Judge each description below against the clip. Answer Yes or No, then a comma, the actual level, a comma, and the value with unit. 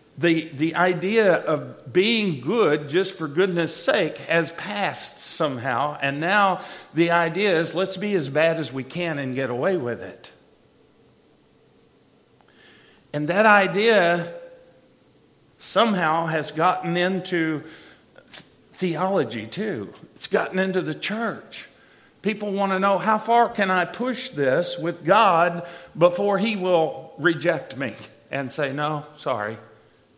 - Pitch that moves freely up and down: No, average, 3.6 semitones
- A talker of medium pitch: Yes, medium, 175 Hz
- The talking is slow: Yes, slow, 130 wpm